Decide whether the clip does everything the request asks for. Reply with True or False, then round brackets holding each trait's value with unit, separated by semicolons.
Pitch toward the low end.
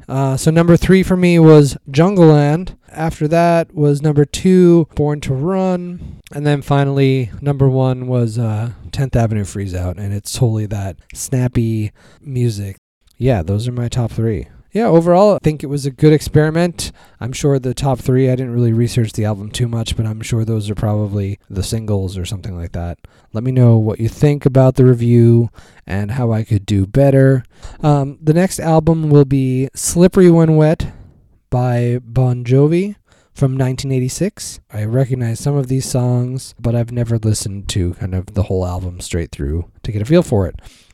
True (125 Hz)